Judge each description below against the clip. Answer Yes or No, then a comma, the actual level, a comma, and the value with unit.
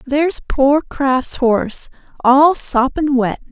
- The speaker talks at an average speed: No, slow, 120 wpm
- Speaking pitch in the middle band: No, very high, 270 Hz